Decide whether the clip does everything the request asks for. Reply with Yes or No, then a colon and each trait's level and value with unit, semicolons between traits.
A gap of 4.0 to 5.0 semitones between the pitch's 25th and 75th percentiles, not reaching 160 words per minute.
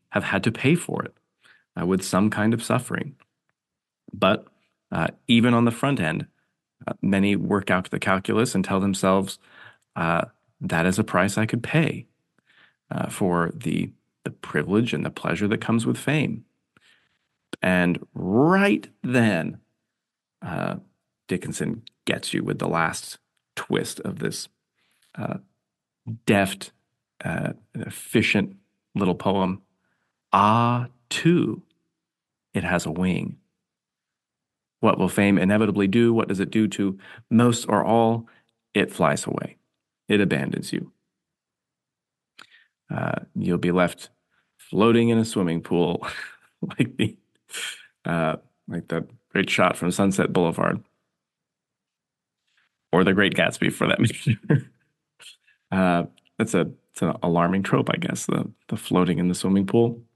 No: average, 3.6 semitones; slow, 135 wpm